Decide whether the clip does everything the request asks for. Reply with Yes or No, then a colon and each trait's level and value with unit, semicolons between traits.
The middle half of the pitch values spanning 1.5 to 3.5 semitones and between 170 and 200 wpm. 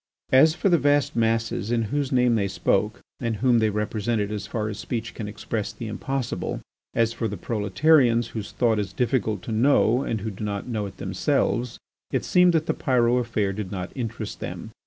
Yes: average, 2.9 semitones; average, 195 wpm